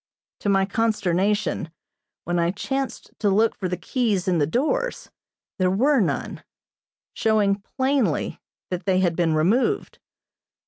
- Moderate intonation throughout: Yes, average, 4.3 semitones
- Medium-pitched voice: No, high, 200 Hz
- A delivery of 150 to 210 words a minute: No, slow, 135 wpm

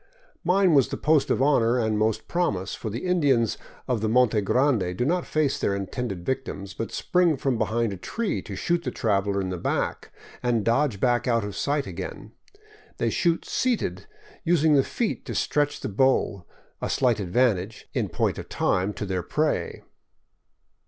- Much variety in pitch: Yes, wide, 6.2 semitones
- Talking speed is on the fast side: No, average, 180 wpm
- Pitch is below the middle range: Yes, low, 120 Hz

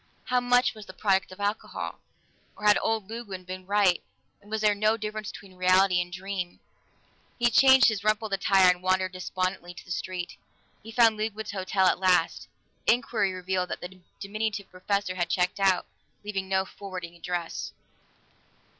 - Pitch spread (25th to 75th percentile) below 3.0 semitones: Yes, narrow, 2.6 semitones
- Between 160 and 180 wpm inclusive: Yes, average, 165 wpm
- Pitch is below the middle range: No, high, 195 Hz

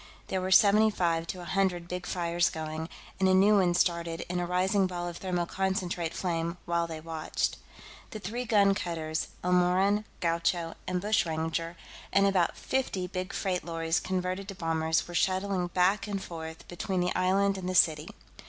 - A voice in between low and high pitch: Yes, medium, 180 Hz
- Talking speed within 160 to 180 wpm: Yes, average, 170 wpm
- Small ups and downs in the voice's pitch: Yes, narrow, 2.3 semitones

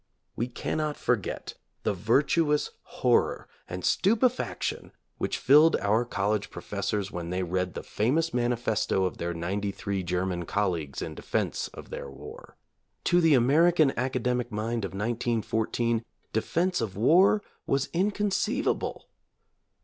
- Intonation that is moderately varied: No, wide, 7.1 semitones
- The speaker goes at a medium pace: No, slow, 125 wpm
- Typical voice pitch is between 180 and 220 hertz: No, low, 115 Hz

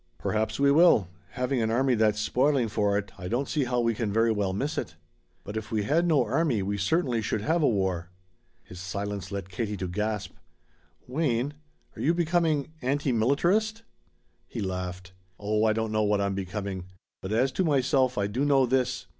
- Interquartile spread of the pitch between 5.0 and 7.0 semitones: Yes, wide, 5.4 semitones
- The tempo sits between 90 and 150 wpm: No, average, 190 wpm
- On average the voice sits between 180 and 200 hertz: No, low, 110 Hz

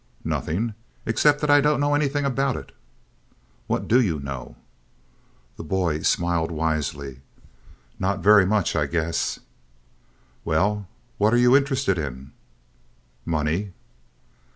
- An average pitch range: No, wide, 8.2 semitones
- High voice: No, very low, 95 Hz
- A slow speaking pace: Yes, slow, 120 wpm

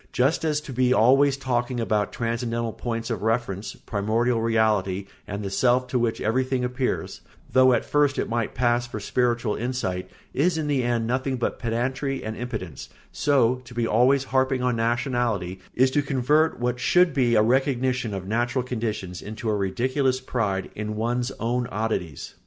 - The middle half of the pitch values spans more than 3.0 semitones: No, narrow, 2.6 semitones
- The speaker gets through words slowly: No, average, 170 wpm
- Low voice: Yes, low, 120 Hz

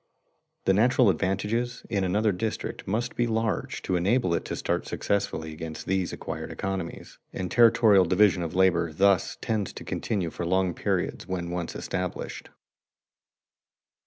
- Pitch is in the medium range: No, very low, 95 Hz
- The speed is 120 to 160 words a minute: Yes, average, 145 wpm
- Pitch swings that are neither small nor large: Yes, average, 3.5 semitones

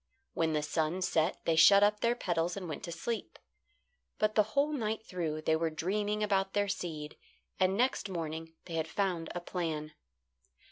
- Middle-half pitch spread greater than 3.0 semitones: Yes, average, 4.2 semitones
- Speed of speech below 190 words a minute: Yes, average, 180 wpm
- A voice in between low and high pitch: Yes, medium, 180 Hz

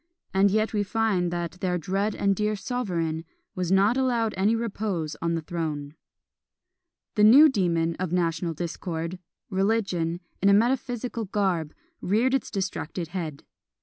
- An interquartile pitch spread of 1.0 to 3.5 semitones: No, average, 4.4 semitones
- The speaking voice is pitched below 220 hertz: Yes, high, 190 Hz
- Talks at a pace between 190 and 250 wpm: No, average, 145 wpm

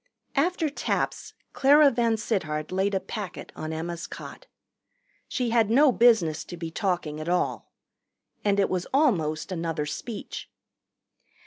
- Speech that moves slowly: Yes, slow, 130 wpm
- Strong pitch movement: Yes, wide, 6.5 semitones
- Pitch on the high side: Yes, high, 195 Hz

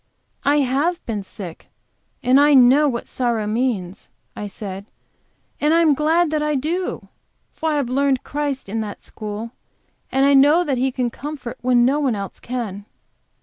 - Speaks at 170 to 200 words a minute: Yes, average, 175 wpm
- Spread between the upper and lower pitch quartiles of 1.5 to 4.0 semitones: No, average, 4.7 semitones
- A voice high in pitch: Yes, very high, 260 Hz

